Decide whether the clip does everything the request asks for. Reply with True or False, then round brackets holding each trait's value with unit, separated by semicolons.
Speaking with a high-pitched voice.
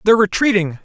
True (200 Hz)